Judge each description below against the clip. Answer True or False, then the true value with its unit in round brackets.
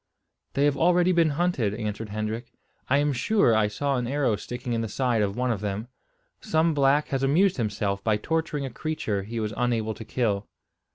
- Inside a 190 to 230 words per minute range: True (195 wpm)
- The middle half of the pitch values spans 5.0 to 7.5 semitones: True (5.3 semitones)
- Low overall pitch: True (120 Hz)